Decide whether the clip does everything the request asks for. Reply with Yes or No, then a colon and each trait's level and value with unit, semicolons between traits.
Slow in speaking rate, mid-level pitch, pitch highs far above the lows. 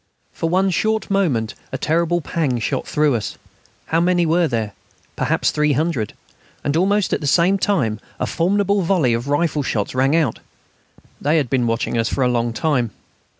No: average, 175 wpm; medium, 150 Hz; wide, 6.1 semitones